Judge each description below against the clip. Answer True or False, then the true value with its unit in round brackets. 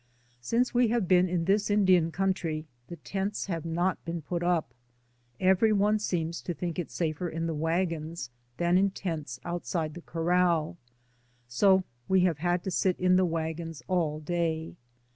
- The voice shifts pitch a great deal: False (2.4 semitones)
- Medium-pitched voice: True (175 Hz)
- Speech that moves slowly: False (165 wpm)